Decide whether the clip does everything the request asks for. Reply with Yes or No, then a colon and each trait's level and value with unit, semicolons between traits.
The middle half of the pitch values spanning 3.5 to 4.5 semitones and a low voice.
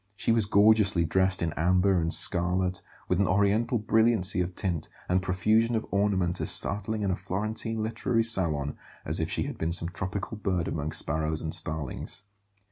Yes: average, 3.8 semitones; very low, 95 Hz